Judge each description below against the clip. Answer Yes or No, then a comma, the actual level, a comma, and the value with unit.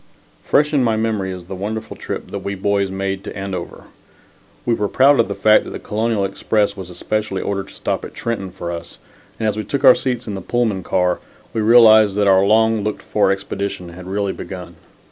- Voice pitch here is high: No, low, 100 Hz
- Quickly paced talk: Yes, fast, 215 wpm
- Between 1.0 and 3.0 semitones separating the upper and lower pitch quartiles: Yes, narrow, 2.5 semitones